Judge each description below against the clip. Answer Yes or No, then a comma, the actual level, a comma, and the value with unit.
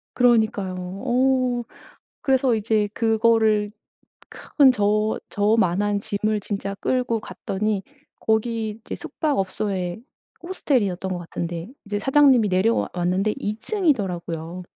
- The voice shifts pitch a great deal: No, average, 3.7 semitones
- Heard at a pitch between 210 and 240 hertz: Yes, high, 215 Hz